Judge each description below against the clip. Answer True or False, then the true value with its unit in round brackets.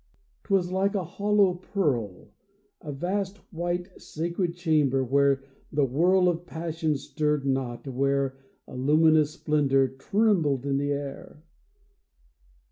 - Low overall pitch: False (155 Hz)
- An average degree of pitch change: True (4.4 semitones)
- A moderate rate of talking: False (125 wpm)